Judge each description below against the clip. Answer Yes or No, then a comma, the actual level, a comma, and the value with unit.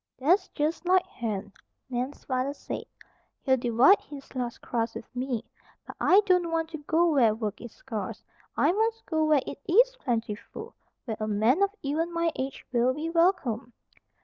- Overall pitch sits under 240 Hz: No, very high, 275 Hz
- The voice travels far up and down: Yes, wide, 6.0 semitones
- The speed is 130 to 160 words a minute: No, average, 175 wpm